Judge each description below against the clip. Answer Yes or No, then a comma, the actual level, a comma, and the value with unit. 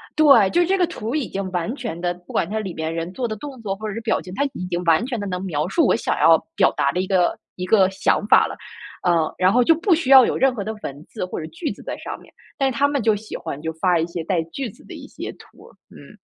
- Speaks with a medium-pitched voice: No, high, 195 Hz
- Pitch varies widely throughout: Yes, wide, 6.1 semitones